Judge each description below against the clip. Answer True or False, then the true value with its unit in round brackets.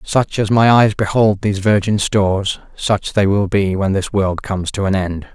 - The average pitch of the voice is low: True (100 Hz)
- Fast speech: True (215 wpm)